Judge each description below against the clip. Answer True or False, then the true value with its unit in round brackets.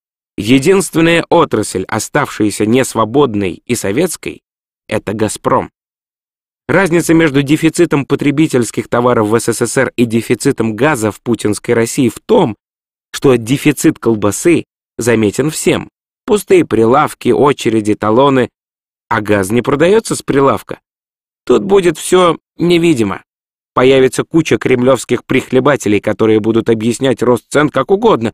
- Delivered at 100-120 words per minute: True (115 wpm)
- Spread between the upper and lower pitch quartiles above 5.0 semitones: True (5.4 semitones)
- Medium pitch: False (125 Hz)